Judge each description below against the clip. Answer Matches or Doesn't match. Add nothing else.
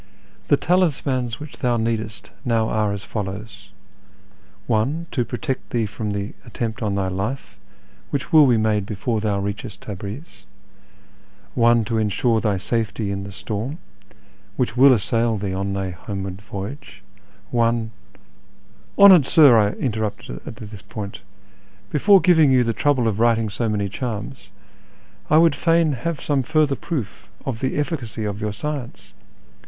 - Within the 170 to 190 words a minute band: Doesn't match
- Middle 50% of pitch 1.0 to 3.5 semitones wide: Doesn't match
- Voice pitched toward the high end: Doesn't match